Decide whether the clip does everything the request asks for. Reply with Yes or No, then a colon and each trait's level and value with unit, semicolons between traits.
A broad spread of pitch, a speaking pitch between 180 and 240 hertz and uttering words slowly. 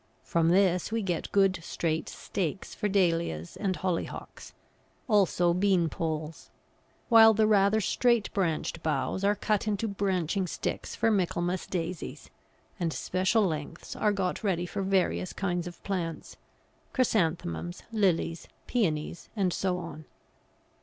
No: average, 3.2 semitones; medium, 185 Hz; slow, 125 wpm